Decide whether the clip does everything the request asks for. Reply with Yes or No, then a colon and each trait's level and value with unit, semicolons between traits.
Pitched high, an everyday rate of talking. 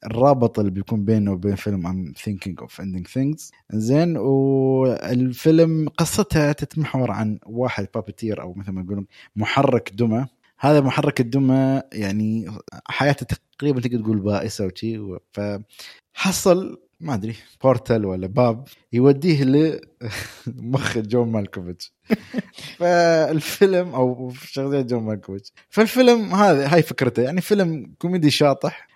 No: low, 125 Hz; average, 120 wpm